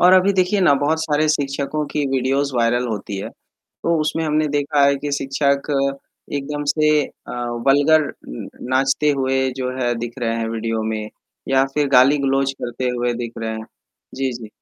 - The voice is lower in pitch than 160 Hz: Yes, low, 135 Hz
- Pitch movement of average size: Yes, average, 3.6 semitones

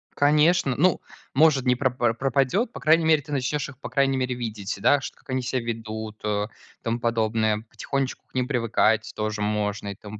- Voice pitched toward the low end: Yes, low, 125 Hz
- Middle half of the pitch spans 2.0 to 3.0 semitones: No, average, 4.1 semitones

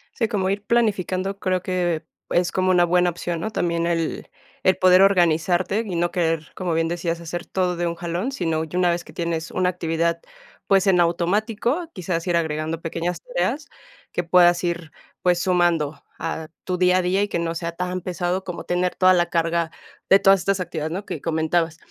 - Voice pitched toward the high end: No, medium, 175 Hz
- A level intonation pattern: Yes, narrow, 1.7 semitones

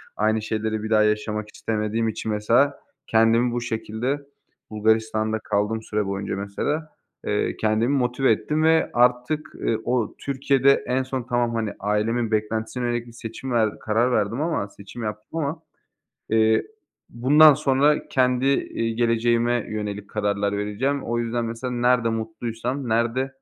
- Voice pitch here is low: Yes, low, 115 Hz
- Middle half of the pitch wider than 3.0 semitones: No, average, 2.7 semitones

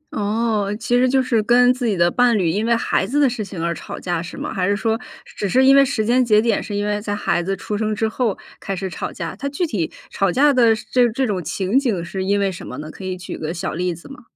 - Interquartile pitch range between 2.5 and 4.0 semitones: No, average, 4.6 semitones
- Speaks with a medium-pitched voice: No, high, 210 Hz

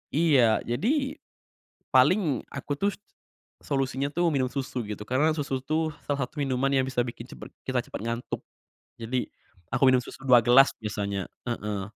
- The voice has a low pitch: Yes, low, 130 Hz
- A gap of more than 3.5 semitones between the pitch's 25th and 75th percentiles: No, average, 3.2 semitones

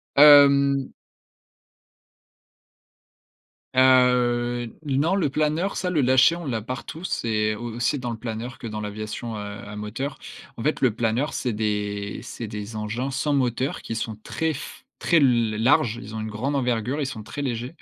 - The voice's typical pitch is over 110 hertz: Yes, low, 120 Hz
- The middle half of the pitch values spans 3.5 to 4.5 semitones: Yes, average, 4.2 semitones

